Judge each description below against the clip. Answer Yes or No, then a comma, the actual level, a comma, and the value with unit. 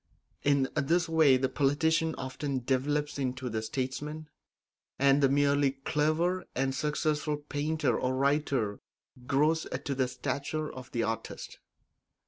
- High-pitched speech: No, medium, 140 Hz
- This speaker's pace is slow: Yes, slow, 125 wpm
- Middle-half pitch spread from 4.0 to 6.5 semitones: No, narrow, 2.6 semitones